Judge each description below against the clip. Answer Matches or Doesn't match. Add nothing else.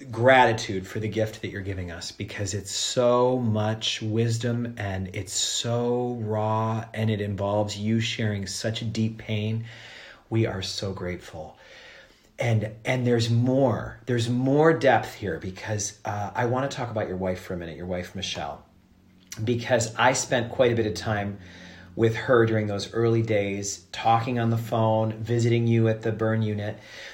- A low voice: Matches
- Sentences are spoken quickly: Doesn't match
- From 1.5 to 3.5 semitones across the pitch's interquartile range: Matches